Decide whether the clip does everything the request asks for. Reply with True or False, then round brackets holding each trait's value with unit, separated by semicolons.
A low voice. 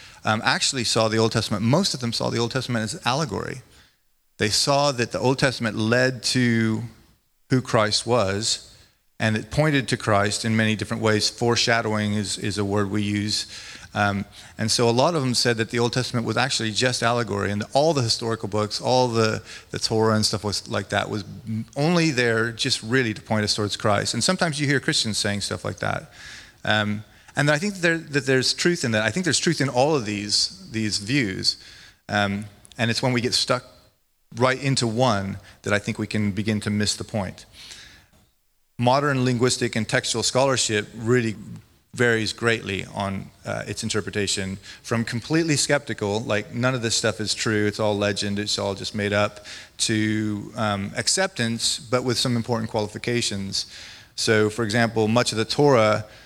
True (110 Hz)